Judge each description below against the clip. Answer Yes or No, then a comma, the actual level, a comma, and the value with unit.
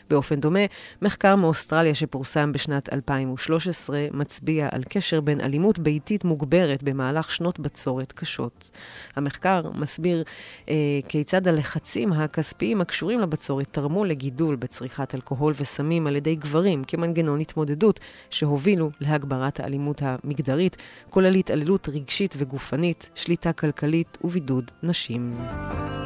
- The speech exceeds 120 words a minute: No, average, 110 wpm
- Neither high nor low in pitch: Yes, medium, 150 Hz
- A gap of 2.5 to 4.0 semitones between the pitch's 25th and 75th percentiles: Yes, average, 3.3 semitones